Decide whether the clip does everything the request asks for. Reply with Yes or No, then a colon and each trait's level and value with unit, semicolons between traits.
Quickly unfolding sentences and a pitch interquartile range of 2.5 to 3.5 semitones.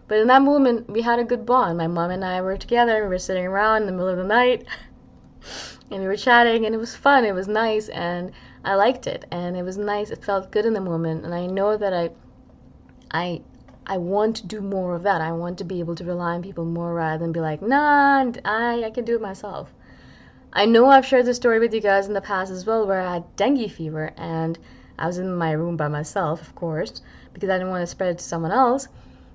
No: fast, 255 wpm; average, 4.5 semitones